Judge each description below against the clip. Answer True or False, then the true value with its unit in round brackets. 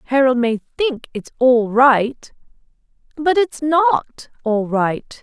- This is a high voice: True (260 Hz)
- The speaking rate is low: True (125 wpm)